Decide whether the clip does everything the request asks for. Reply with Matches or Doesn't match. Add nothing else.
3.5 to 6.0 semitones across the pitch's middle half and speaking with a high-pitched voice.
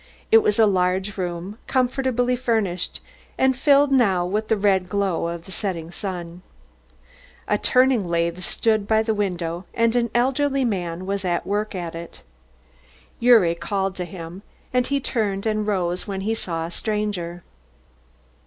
Matches